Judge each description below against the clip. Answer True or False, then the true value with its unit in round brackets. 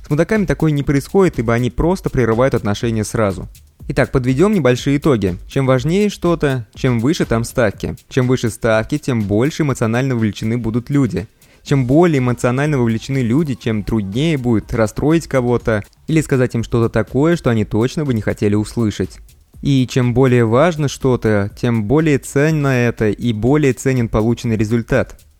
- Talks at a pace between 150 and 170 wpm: True (160 wpm)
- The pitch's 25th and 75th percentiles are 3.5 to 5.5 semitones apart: True (4.1 semitones)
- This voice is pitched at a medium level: False (125 Hz)